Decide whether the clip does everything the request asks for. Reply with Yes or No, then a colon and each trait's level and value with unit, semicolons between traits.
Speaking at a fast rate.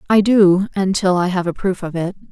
Yes: fast, 235 wpm